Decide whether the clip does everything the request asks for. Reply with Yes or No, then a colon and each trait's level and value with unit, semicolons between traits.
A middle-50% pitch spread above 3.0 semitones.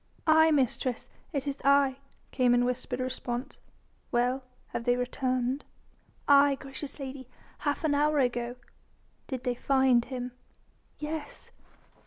No: narrow, 2.4 semitones